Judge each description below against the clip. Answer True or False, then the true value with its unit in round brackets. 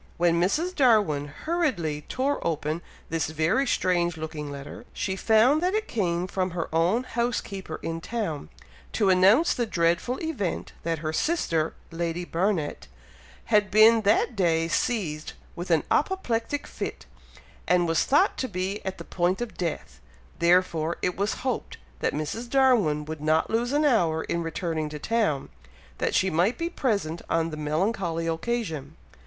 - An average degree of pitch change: False (6.2 semitones)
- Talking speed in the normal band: True (155 wpm)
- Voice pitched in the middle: True (180 Hz)